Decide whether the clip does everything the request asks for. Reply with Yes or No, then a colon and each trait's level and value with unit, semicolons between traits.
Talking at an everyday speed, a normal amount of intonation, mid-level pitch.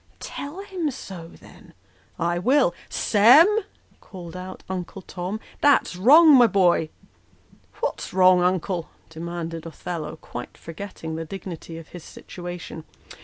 Yes: average, 150 wpm; average, 3.7 semitones; medium, 180 Hz